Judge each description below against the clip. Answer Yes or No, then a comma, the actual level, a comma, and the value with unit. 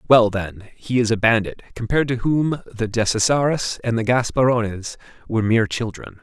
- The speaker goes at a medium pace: Yes, average, 165 wpm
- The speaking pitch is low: Yes, low, 115 Hz